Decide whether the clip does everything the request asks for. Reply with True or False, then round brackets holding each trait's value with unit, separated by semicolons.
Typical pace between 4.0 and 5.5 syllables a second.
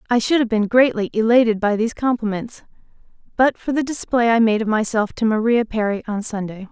False (5.8 syllables/s)